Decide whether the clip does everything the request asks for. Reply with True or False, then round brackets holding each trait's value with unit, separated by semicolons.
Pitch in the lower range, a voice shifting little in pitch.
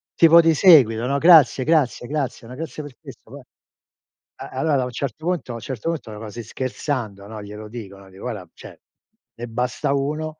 False (130 Hz; 5.4 semitones)